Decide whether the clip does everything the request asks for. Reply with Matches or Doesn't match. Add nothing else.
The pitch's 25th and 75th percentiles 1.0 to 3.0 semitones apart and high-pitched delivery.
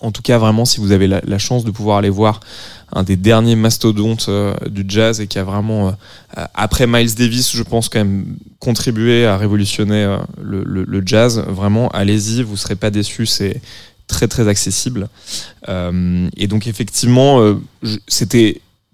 Doesn't match